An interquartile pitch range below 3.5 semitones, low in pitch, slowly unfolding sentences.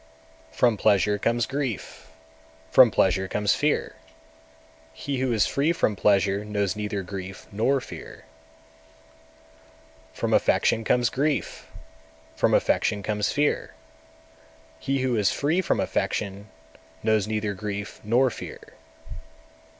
No: average, 4.2 semitones; low, 105 Hz; slow, 120 wpm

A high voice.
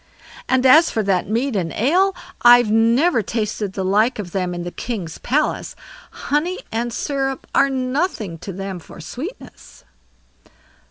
Yes: high, 230 Hz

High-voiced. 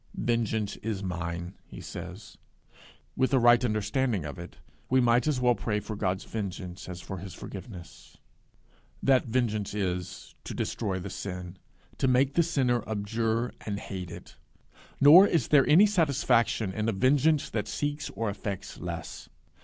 No: low, 110 Hz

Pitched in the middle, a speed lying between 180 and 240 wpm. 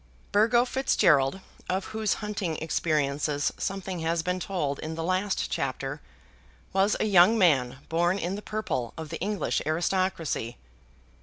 No: medium, 175 Hz; average, 140 wpm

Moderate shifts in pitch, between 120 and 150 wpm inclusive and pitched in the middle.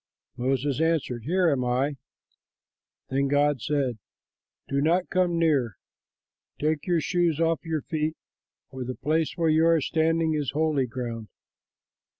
Yes: average, 3.6 semitones; average, 140 wpm; medium, 150 Hz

